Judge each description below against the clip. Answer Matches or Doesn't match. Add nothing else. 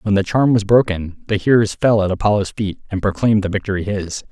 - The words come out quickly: Matches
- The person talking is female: Doesn't match